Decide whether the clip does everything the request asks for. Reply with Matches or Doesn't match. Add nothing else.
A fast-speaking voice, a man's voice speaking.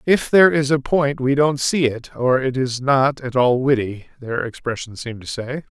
Matches